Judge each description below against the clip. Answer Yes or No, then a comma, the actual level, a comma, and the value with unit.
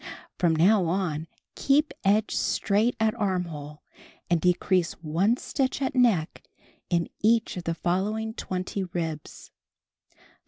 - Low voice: No, medium, 185 Hz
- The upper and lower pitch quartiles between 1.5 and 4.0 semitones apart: No, average, 4.7 semitones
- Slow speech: Yes, slow, 120 wpm